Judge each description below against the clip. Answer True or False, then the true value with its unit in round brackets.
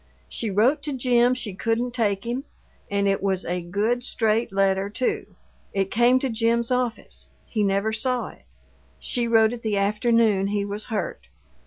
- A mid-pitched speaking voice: False (220 Hz)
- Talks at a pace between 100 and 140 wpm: False (170 wpm)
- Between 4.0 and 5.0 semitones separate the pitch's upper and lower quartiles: False (3.2 semitones)